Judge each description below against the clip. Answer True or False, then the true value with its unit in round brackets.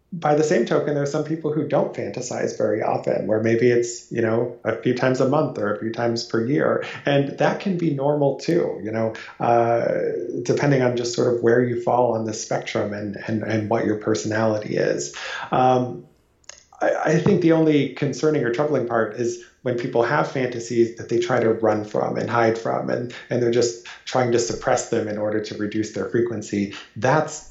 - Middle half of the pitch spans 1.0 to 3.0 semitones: False (4.2 semitones)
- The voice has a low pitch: True (120 Hz)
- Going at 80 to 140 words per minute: False (205 wpm)